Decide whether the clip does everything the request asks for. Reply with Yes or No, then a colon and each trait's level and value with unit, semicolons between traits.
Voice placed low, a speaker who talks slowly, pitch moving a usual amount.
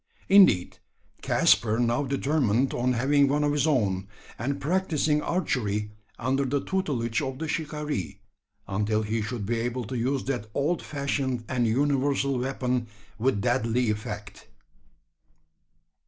Yes: low, 130 Hz; slow, 130 wpm; average, 3.9 semitones